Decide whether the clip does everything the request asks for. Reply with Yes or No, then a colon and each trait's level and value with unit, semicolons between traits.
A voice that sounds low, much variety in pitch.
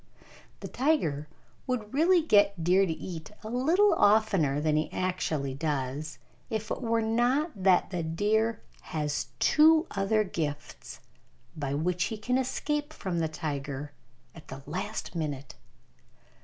No: medium, 185 Hz; wide, 6.9 semitones